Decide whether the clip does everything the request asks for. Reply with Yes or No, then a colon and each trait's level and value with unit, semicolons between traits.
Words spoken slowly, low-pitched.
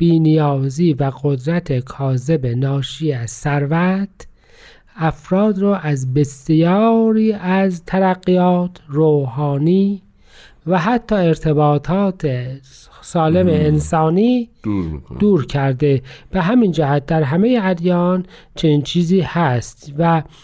No: slow, 90 wpm; medium, 160 Hz